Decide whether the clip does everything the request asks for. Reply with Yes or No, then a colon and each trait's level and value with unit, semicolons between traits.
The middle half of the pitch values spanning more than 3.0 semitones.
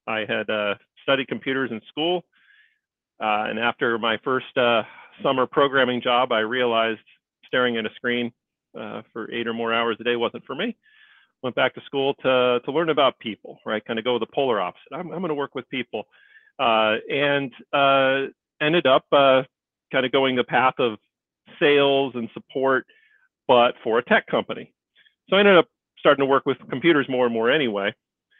Yes: average, 3.4 semitones